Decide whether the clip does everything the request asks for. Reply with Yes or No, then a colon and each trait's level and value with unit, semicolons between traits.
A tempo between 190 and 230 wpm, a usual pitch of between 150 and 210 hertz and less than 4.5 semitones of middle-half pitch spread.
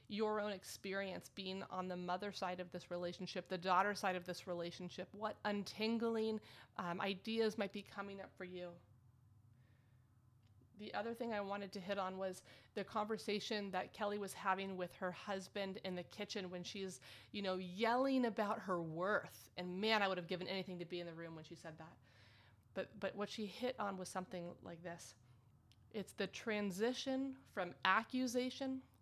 No: average, 180 wpm; high, 190 Hz; average, 2.8 semitones